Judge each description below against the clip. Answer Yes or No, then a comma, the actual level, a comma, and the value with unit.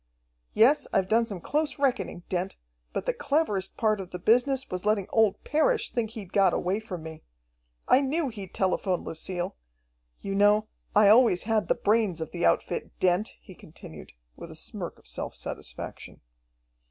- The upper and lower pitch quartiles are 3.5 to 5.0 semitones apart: Yes, average, 4.2 semitones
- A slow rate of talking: No, average, 170 wpm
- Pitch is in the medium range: No, high, 205 Hz